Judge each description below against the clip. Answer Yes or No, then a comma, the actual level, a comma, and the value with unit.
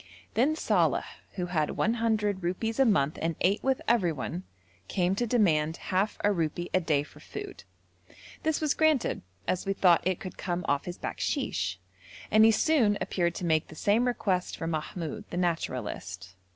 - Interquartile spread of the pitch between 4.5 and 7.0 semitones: Yes, wide, 5.5 semitones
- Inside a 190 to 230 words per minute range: No, average, 170 wpm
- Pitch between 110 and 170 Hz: No, medium, 180 Hz